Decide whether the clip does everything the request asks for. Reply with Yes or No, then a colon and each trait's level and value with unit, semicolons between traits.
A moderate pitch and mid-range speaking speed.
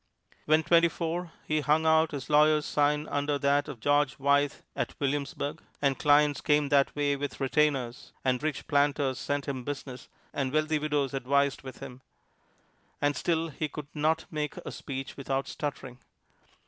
Yes: medium, 145 Hz; average, 160 wpm